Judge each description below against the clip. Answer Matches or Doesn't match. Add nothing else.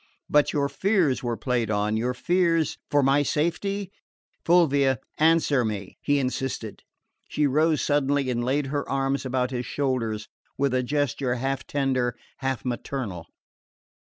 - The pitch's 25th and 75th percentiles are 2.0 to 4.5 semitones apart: Matches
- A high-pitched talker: Doesn't match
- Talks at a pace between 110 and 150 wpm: Matches